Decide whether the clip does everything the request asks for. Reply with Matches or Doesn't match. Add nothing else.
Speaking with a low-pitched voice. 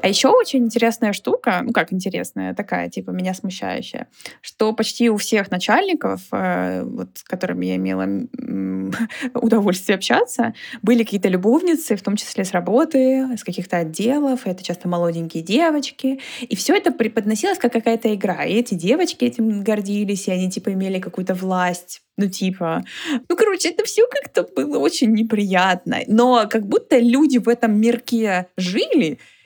Doesn't match